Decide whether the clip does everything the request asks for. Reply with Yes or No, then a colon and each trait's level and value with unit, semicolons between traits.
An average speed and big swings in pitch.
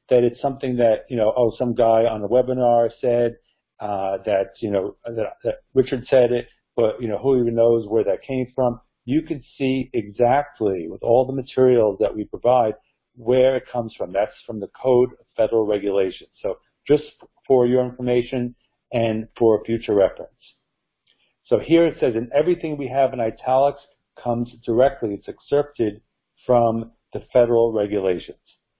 No: average, 170 wpm; narrow, 2.4 semitones